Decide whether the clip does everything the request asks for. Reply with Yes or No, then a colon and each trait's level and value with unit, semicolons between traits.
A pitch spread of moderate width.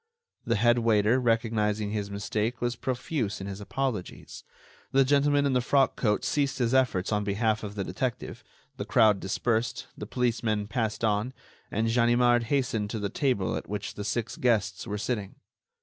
Yes: average, 3.1 semitones